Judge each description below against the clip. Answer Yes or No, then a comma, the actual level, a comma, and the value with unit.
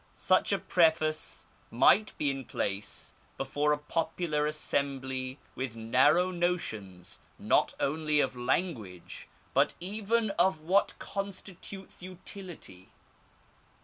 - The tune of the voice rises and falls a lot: Yes, wide, 5.7 semitones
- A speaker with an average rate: No, slow, 105 wpm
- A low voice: No, medium, 155 Hz